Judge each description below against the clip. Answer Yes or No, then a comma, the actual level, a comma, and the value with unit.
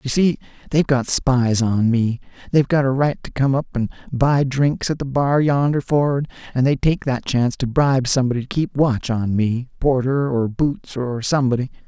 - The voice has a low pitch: Yes, low, 130 Hz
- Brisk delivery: No, average, 195 wpm